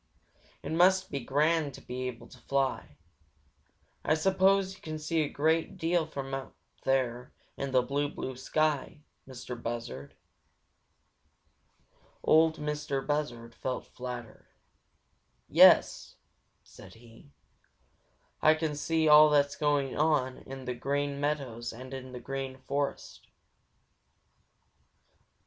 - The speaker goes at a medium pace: No, slow, 125 wpm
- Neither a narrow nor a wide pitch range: Yes, average, 3.3 semitones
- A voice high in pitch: No, medium, 140 Hz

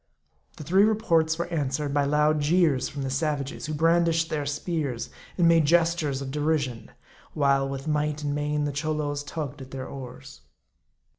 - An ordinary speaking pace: Yes, average, 165 wpm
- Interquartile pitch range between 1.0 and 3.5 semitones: Yes, narrow, 2.5 semitones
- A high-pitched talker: No, medium, 150 Hz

